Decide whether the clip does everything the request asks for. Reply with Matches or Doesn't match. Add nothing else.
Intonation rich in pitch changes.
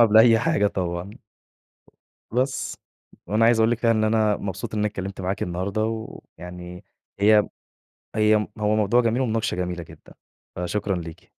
Doesn't match